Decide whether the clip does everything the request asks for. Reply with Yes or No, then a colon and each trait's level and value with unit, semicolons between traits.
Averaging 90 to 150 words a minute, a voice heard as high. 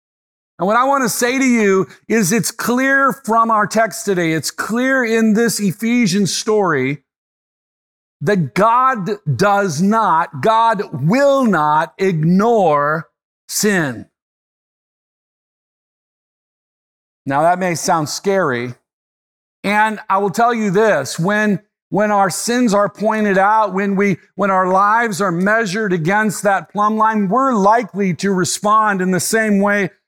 Yes: slow, 135 wpm; high, 205 Hz